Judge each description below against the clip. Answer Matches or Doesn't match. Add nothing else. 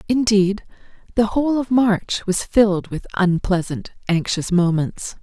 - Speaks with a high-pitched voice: Matches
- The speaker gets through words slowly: Matches